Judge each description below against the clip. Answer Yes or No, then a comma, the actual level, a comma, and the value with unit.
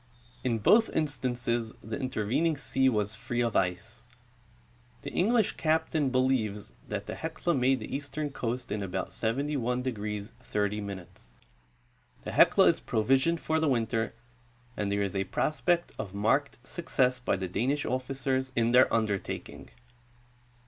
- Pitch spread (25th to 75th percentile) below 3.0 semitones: No, average, 4.3 semitones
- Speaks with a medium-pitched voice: No, low, 125 Hz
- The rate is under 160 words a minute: Yes, slow, 135 wpm